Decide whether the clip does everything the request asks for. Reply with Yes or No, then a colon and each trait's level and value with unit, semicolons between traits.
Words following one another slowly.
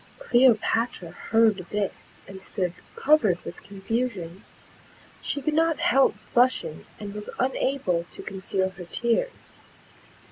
Yes: slow, 115 wpm